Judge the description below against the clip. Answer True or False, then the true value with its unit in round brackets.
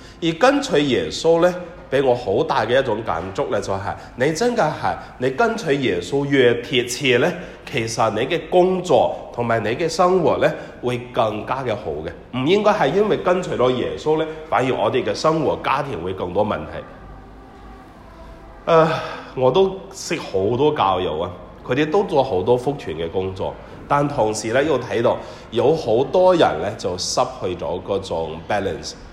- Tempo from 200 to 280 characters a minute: True (250 characters per minute)